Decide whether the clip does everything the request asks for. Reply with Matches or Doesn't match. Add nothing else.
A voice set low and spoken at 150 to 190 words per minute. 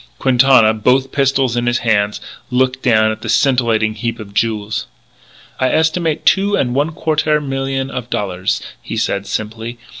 Matches